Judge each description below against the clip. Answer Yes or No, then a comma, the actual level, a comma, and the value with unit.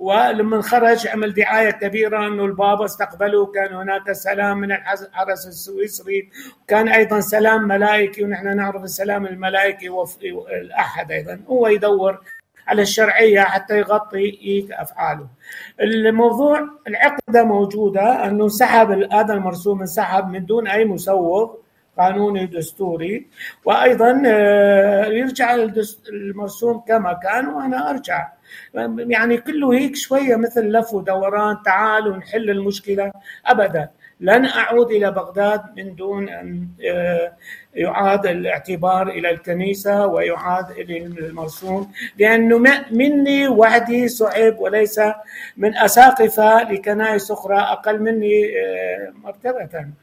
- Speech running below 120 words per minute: Yes, average, 105 wpm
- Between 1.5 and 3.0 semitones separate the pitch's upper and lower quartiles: Yes, narrow, 2.4 semitones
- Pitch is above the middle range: Yes, high, 205 Hz